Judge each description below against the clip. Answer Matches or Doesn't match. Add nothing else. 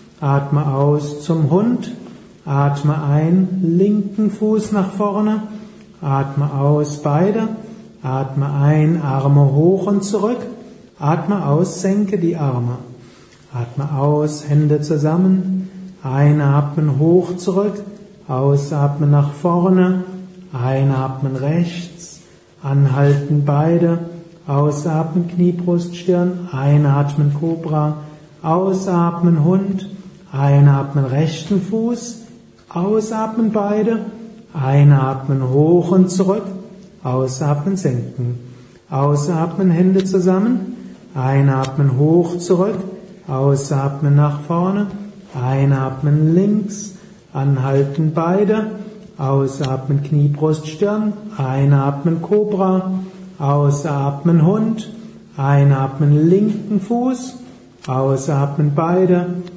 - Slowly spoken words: Matches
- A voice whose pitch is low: Doesn't match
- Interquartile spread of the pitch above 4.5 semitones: Matches